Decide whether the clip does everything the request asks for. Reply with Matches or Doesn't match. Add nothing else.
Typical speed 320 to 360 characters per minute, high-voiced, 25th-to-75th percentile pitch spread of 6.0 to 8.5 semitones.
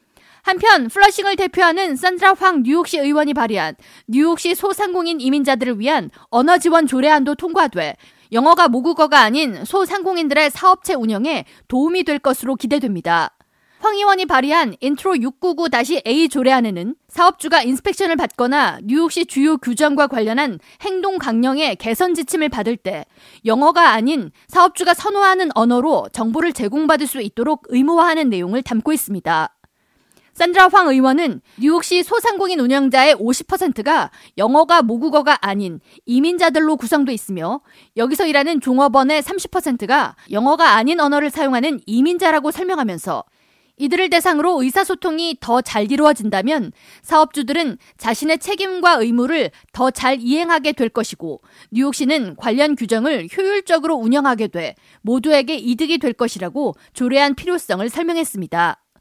Doesn't match